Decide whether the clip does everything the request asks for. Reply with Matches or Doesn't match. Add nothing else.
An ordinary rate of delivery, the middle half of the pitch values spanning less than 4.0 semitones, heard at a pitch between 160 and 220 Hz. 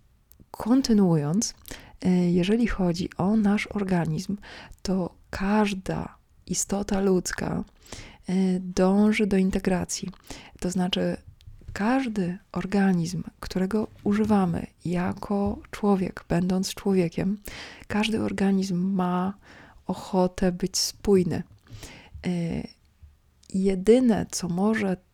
Doesn't match